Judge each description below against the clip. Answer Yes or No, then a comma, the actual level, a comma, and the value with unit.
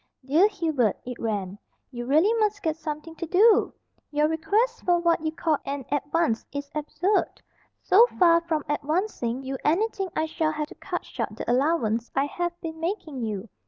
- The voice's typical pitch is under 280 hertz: No, very high, 315 Hz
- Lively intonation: No, average, 4.2 semitones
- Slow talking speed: No, average, 175 wpm